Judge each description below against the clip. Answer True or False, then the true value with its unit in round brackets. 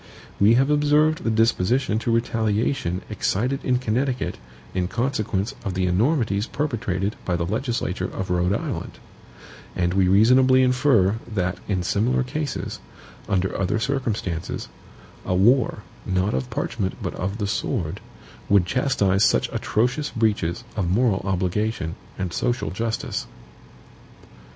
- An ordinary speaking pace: False (130 wpm)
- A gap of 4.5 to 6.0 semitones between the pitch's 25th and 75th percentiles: True (5.1 semitones)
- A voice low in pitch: True (105 Hz)